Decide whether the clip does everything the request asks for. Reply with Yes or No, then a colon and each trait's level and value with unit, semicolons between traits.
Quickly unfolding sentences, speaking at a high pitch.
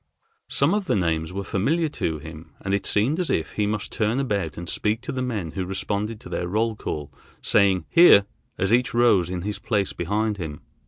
No: fast, 210 wpm; low, 100 Hz